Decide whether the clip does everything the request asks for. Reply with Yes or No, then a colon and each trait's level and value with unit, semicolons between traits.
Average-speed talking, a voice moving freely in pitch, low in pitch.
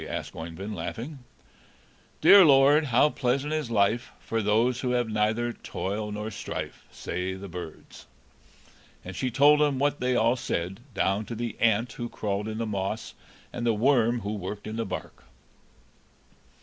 No: average, 160 wpm; average, 3.6 semitones; low, 115 Hz